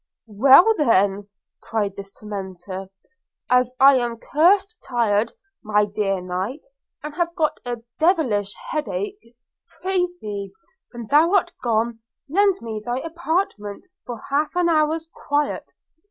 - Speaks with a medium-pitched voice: No, high, 240 Hz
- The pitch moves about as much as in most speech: No, wide, 7.7 semitones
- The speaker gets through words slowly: Yes, slow, 125 wpm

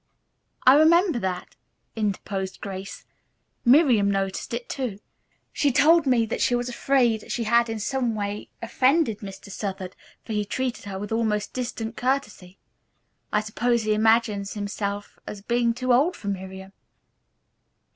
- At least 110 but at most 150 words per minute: Yes, average, 145 wpm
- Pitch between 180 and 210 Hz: No, high, 225 Hz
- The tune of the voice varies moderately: Yes, average, 3.7 semitones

